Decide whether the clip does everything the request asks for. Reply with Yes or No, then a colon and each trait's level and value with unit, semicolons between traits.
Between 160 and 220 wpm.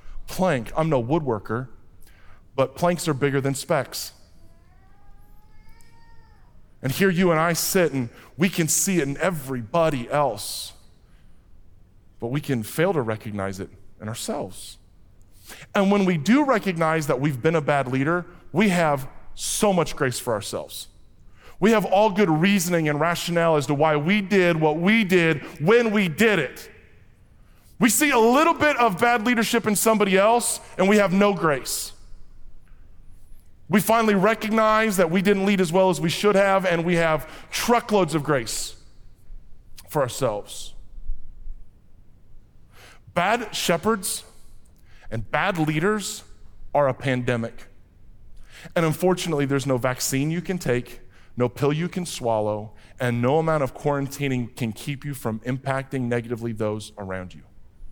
No: average, 145 wpm